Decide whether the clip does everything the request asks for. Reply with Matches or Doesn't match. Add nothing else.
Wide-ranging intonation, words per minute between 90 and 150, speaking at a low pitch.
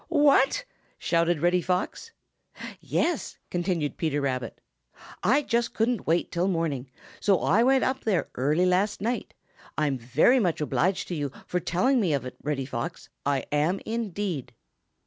Doesn't match